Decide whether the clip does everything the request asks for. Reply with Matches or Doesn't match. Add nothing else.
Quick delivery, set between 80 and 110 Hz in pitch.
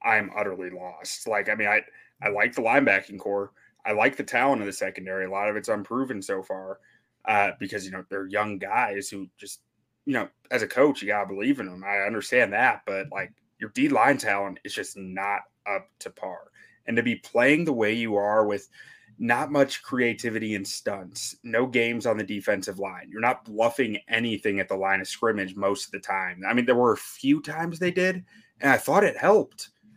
Matches